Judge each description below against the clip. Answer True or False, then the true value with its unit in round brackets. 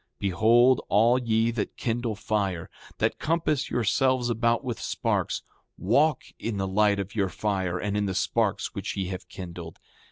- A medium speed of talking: True (165 wpm)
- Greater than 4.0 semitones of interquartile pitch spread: False (3.7 semitones)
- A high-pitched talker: False (105 Hz)